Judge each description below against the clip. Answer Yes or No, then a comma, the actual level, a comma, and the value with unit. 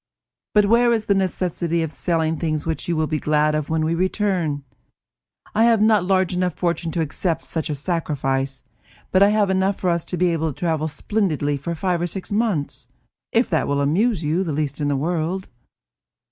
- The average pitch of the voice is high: No, medium, 170 Hz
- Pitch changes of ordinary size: Yes, average, 3.7 semitones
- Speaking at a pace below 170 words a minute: No, fast, 205 wpm